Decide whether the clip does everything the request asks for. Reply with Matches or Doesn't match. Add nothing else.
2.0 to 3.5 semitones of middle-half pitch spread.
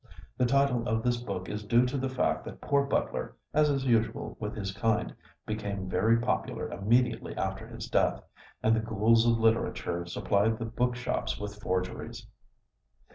Matches